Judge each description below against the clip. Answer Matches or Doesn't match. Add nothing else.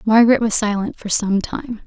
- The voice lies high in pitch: Matches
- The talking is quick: Doesn't match